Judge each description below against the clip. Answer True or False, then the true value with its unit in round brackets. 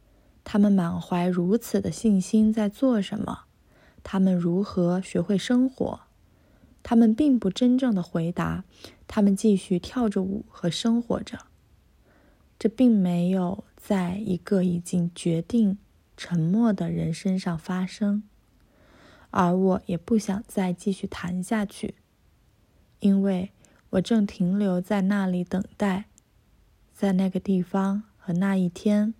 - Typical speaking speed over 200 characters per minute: False (185 characters per minute)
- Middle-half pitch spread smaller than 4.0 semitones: True (2.9 semitones)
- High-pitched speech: True (195 Hz)